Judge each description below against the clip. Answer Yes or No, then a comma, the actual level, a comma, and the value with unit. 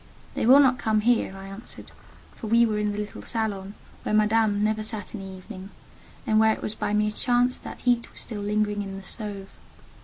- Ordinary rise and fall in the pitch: No, narrow, 1.7 semitones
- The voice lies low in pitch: No, high, 215 Hz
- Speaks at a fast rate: Yes, fast, 215 wpm